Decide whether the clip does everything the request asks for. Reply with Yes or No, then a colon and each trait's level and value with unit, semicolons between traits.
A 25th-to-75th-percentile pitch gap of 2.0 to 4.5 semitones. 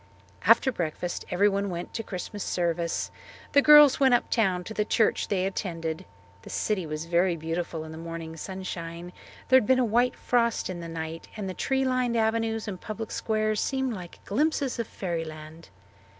No: wide, 5.4 semitones